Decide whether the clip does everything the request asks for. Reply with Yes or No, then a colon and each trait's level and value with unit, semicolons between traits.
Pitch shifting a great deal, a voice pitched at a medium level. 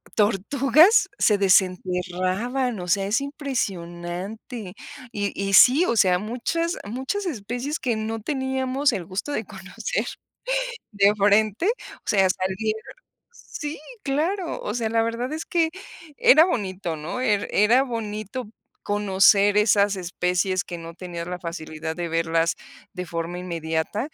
No: wide, 5.8 semitones; high, 205 Hz